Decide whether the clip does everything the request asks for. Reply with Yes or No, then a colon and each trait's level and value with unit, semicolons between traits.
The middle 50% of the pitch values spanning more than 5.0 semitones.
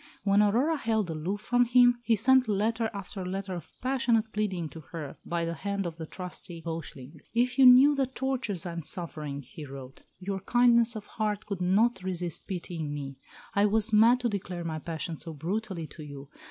Yes: wide, 5.5 semitones